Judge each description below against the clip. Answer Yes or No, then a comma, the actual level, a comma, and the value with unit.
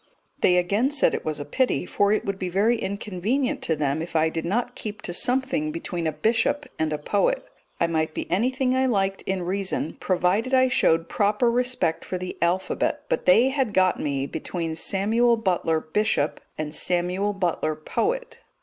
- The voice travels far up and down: Yes, wide, 6.3 semitones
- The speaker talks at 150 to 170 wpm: No, average, 185 wpm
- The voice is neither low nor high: No, high, 195 Hz